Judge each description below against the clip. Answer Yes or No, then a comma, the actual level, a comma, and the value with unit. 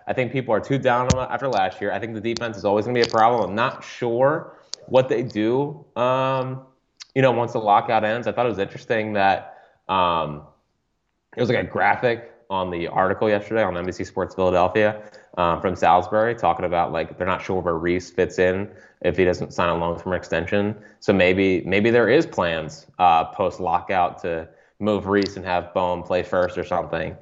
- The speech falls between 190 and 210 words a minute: Yes, fast, 205 wpm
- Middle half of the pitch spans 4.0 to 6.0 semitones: Yes, average, 4.4 semitones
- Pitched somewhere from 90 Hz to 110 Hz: Yes, low, 100 Hz